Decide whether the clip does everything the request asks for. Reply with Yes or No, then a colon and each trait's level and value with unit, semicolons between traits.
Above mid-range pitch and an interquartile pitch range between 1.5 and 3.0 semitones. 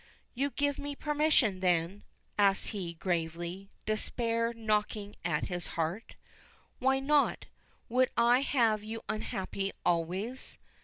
No: high, 215 Hz; wide, 5.5 semitones